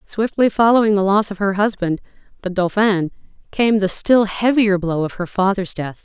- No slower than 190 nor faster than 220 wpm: No, average, 180 wpm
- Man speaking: No, female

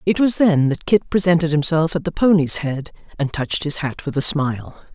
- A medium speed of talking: No, fast, 220 wpm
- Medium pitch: Yes, medium, 160 Hz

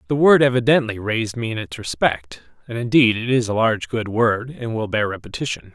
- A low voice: Yes, low, 115 Hz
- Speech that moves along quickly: Yes, fast, 210 wpm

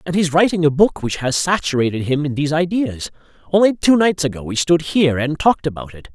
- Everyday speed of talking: No, fast, 225 wpm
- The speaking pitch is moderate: Yes, medium, 155 Hz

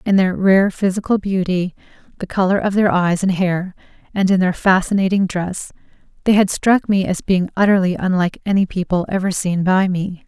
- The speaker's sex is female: Yes, female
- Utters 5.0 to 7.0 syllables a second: Yes, 5.2 syllables/s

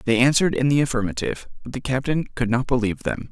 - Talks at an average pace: No, fast, 215 wpm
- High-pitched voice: No, low, 130 Hz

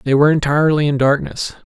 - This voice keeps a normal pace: Yes, average, 175 wpm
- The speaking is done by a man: Yes, male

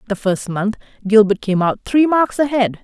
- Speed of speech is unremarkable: Yes, average, 190 wpm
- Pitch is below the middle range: No, high, 220 Hz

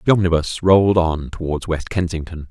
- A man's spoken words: Yes, male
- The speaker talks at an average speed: Yes, average, 170 wpm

